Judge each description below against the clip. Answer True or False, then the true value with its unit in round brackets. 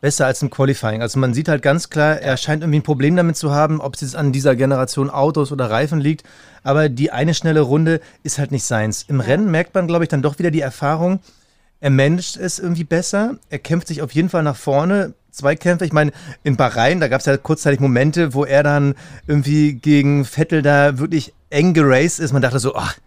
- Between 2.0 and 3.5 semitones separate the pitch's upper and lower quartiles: True (2.8 semitones)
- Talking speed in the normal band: False (235 wpm)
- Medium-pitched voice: True (145 Hz)